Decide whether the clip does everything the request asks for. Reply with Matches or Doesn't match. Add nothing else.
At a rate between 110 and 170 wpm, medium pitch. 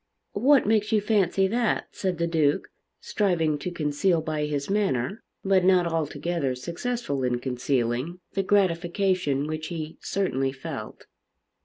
Matches